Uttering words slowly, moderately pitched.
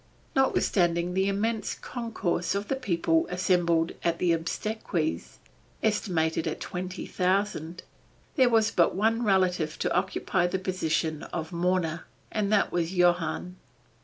Yes: slow, 125 wpm; medium, 180 Hz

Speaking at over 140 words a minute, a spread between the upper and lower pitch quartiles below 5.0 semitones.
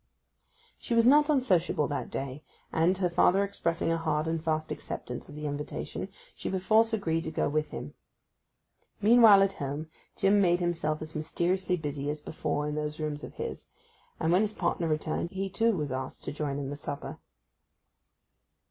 Yes: average, 175 wpm; average, 4.4 semitones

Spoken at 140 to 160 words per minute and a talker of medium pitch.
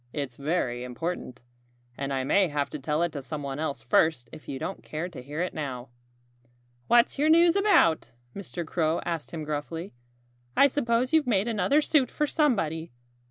No: average, 175 wpm; medium, 160 Hz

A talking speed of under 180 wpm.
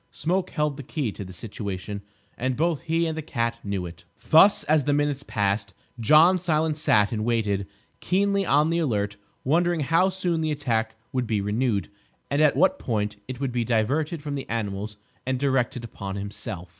No: average, 185 wpm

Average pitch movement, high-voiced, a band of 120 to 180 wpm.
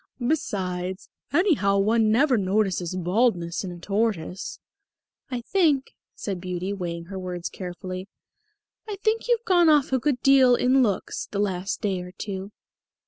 No: wide, 6.0 semitones; high, 200 Hz; average, 145 wpm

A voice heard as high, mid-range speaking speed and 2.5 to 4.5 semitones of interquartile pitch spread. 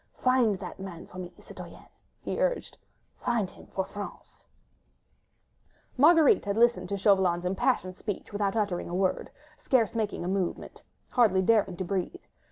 Yes: high, 200 Hz; average, 150 wpm; average, 3.8 semitones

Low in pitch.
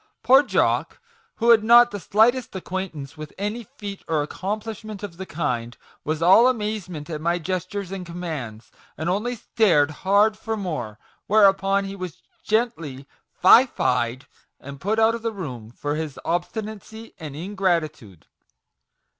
No: high, 190 Hz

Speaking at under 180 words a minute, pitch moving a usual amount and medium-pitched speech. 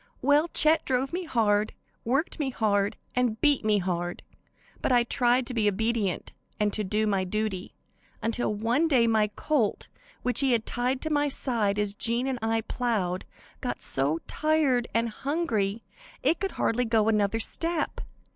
No: average, 165 wpm; average, 4.2 semitones; high, 230 Hz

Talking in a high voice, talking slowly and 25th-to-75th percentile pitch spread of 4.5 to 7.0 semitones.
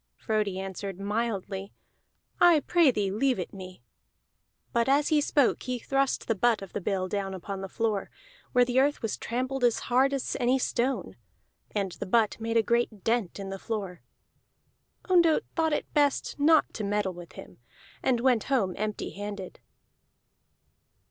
No: high, 225 Hz; average, 165 wpm; average, 5.1 semitones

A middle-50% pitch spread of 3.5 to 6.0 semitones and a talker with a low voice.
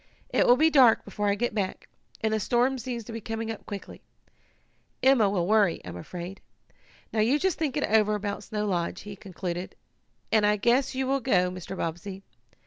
No: average, 3.9 semitones; high, 215 Hz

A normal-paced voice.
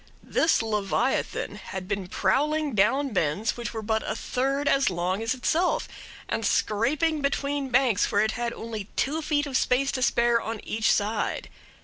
Yes: average, 165 wpm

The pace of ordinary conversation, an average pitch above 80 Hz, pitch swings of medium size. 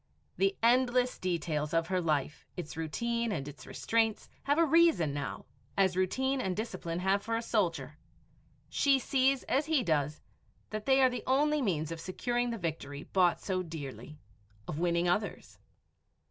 No: average, 160 wpm; high, 190 Hz; wide, 7.3 semitones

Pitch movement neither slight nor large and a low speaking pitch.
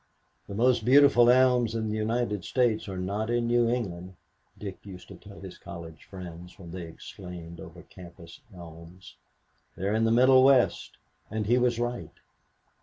Yes: average, 4.9 semitones; low, 105 Hz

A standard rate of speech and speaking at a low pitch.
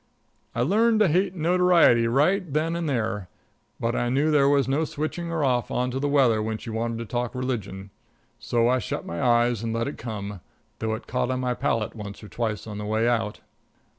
No: fast, 215 wpm; low, 120 Hz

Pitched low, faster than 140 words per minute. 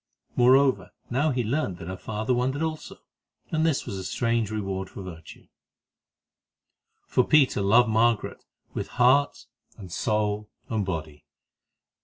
No: low, 110 Hz; slow, 135 wpm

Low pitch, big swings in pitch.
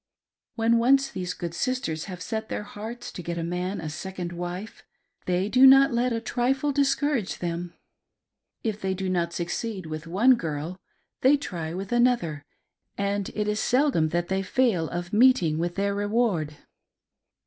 No: high, 195 Hz; wide, 5.7 semitones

